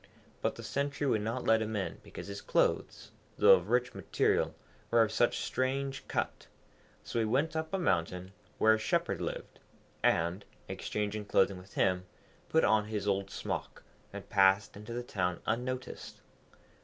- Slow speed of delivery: No, average, 165 wpm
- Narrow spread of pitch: No, average, 4.2 semitones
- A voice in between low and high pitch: No, low, 110 Hz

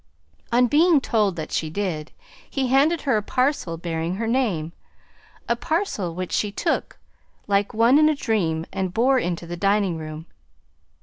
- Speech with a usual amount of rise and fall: No, wide, 7.2 semitones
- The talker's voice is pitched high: Yes, high, 205 Hz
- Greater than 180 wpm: No, average, 165 wpm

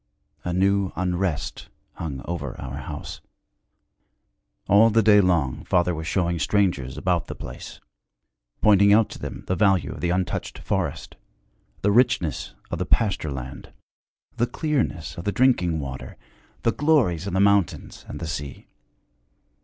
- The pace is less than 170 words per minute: Yes, average, 145 wpm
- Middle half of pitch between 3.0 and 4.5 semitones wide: Yes, average, 4.2 semitones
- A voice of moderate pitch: No, very low, 90 Hz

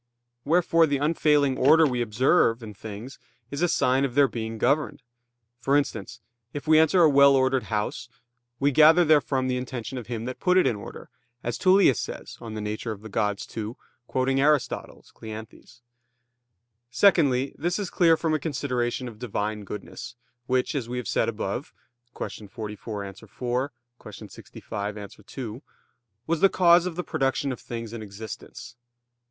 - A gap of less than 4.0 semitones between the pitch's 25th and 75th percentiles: No, average, 5.0 semitones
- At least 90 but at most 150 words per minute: No, average, 165 wpm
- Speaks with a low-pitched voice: Yes, low, 130 Hz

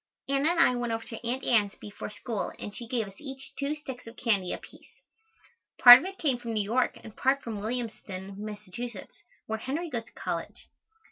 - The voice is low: No, high, 235 Hz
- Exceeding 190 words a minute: Yes, average, 200 wpm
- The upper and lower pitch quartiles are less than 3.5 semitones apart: No, average, 3.8 semitones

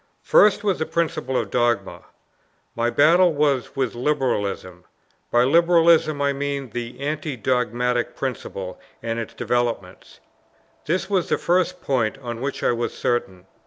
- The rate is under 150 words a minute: Yes, average, 140 wpm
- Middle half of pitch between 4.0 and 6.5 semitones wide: Yes, average, 4.7 semitones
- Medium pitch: No, low, 130 Hz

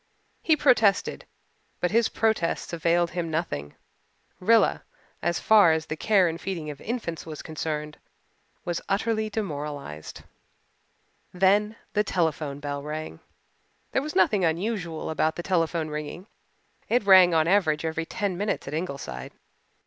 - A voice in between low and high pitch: Yes, medium, 170 Hz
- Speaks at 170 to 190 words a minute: No, average, 140 wpm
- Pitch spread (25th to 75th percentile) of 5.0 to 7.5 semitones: No, average, 4.5 semitones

